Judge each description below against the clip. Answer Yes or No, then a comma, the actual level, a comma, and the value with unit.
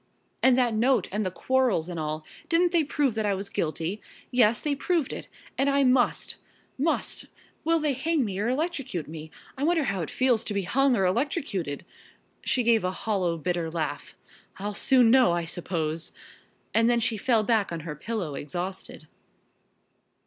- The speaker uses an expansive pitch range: Yes, wide, 7.0 semitones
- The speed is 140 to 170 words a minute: No, average, 180 wpm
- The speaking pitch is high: Yes, high, 220 Hz